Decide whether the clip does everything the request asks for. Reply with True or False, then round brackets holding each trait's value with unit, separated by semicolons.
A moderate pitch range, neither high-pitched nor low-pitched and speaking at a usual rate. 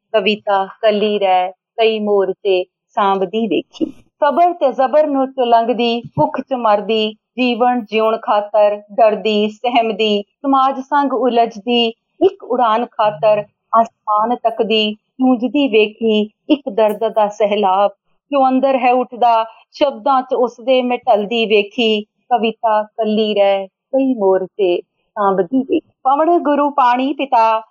False (3.7 semitones; 225 Hz; 125 wpm)